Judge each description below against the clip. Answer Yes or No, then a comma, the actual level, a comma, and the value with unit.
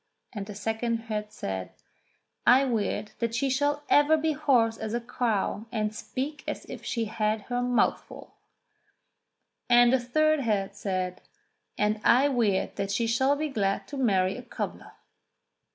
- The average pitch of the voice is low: No, high, 230 Hz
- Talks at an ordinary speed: Yes, average, 160 wpm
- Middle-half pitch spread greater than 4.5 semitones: No, average, 3.9 semitones